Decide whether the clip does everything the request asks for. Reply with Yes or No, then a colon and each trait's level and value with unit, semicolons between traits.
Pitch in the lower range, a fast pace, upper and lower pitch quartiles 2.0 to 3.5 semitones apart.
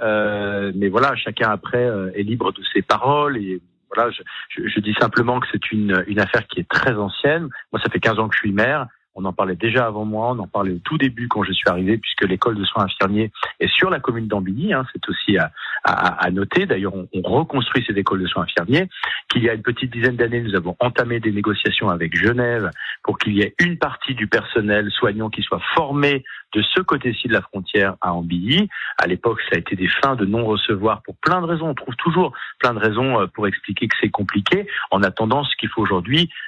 No: low, 110 Hz; fast, 230 wpm; average, 4.0 semitones